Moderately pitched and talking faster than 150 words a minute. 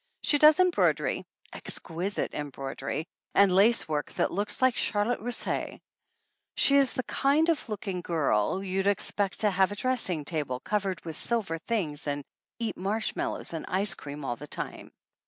No: high, 195 Hz; average, 160 wpm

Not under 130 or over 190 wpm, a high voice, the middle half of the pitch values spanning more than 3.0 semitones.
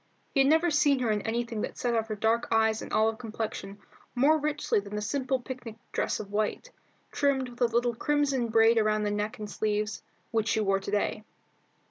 No: fast, 205 wpm; high, 225 Hz; average, 3.4 semitones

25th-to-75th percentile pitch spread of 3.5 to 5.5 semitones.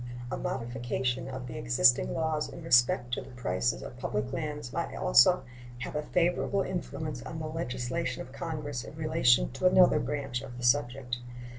Yes: average, 3.8 semitones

